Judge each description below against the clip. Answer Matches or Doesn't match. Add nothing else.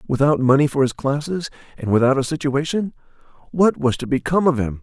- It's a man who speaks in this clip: Matches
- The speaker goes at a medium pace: Matches